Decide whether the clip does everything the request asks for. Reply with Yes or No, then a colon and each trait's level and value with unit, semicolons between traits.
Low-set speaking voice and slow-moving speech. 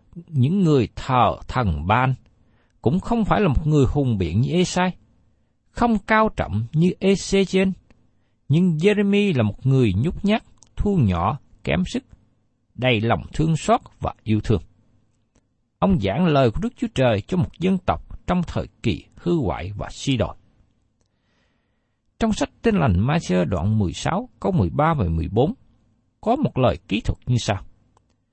Yes: low, 125 Hz; slow, 160 wpm